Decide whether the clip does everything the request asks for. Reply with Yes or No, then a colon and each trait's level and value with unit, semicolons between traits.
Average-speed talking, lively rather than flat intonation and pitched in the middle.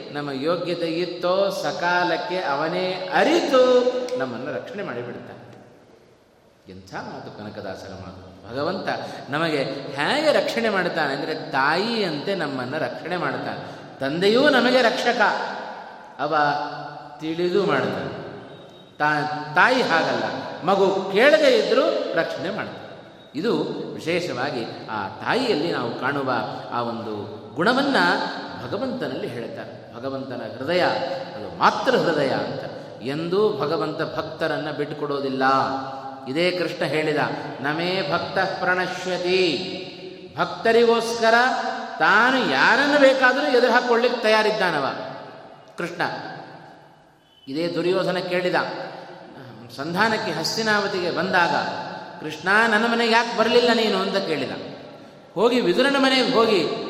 Yes: average, 95 wpm; wide, 7.0 semitones; medium, 175 Hz